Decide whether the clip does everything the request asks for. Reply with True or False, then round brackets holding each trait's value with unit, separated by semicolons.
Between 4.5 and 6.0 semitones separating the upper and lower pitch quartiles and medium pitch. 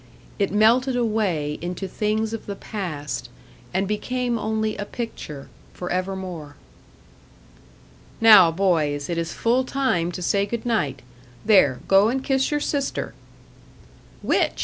False (5.0 semitones; 200 Hz)